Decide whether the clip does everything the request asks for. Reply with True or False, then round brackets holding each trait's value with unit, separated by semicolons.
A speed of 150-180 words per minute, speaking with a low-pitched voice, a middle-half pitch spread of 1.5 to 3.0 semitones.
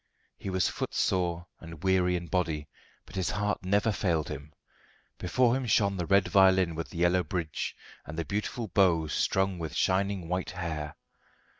True (165 wpm; 90 Hz; 2.7 semitones)